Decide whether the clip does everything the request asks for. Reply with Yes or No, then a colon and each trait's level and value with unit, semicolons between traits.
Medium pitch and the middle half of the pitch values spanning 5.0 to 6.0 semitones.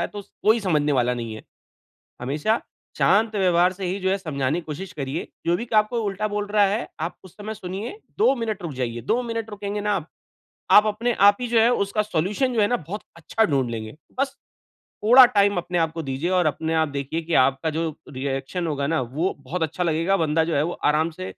Yes: medium, 180 Hz; wide, 5.5 semitones